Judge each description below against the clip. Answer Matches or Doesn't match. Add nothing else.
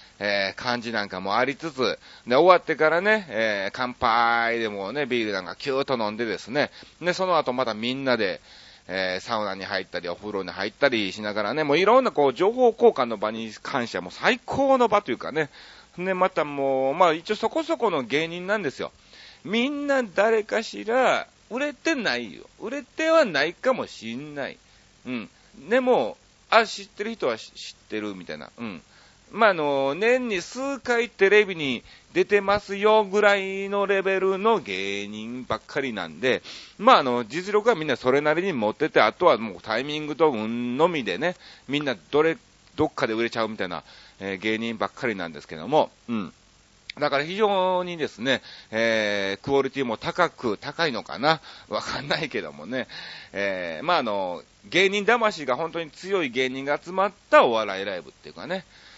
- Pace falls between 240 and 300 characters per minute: Doesn't match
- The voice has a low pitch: Doesn't match